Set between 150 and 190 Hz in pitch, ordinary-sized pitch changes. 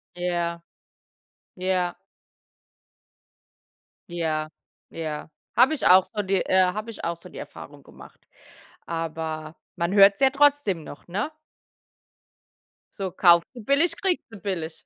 Yes: medium, 185 Hz; average, 4.2 semitones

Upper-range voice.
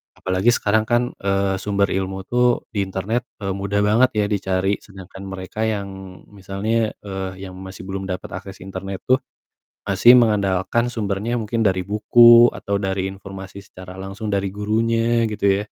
No: low, 100 Hz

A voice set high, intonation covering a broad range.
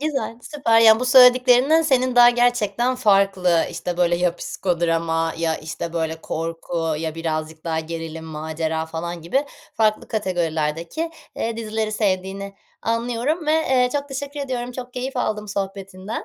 Yes: high, 200 Hz; wide, 7.0 semitones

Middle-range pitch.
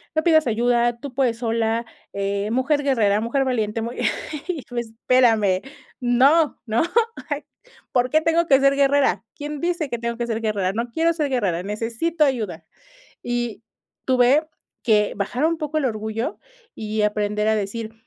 No: high, 240 Hz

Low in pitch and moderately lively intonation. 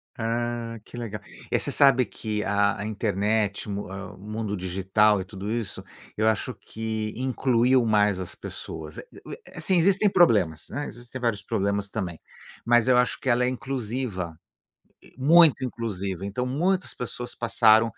Yes: low, 110 Hz; average, 3.6 semitones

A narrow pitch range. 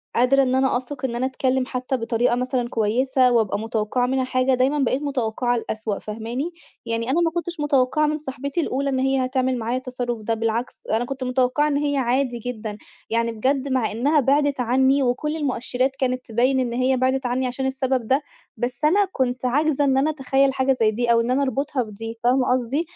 Yes: narrow, 2.1 semitones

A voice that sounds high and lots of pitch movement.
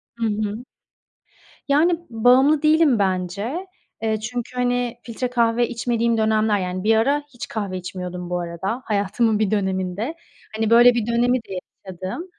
No: high, 225 Hz; average, 3.7 semitones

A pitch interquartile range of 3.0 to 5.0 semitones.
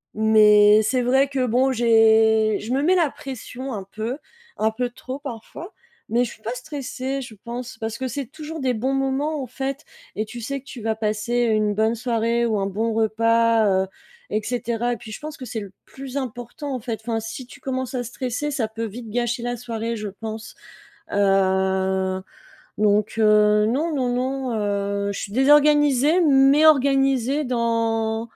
Yes: average, 3.4 semitones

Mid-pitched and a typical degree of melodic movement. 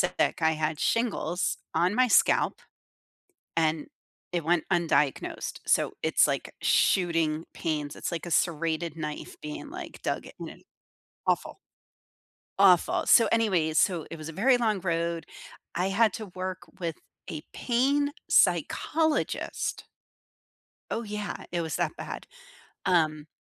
Yes: medium, 170 Hz; average, 4.3 semitones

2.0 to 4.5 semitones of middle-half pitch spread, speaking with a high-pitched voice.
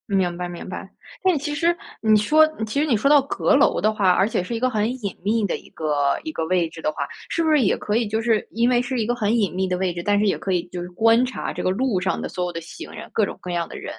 No: average, 5.1 semitones; high, 210 Hz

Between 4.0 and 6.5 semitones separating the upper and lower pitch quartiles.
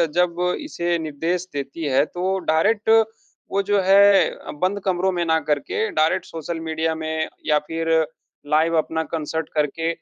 No: average, 2.9 semitones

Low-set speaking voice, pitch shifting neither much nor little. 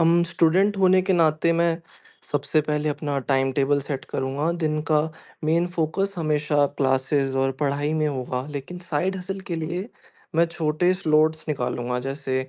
No: medium, 155 Hz; average, 3.2 semitones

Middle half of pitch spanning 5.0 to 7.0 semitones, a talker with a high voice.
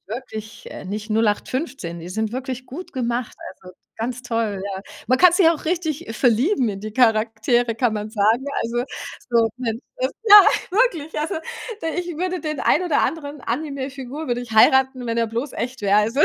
Yes: average, 5.3 semitones; high, 245 Hz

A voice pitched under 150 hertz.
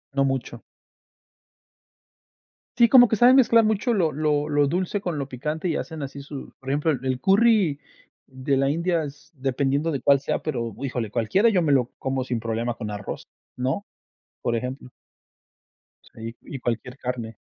Yes: medium, 140 Hz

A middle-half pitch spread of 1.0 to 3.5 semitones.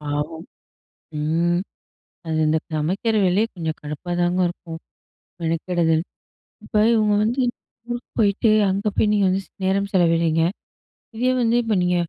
No: average, 3.9 semitones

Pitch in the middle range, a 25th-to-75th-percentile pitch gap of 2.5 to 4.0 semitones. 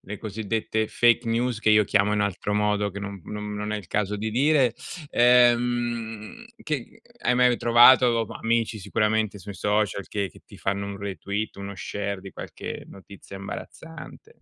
No: low, 105 Hz; average, 2.8 semitones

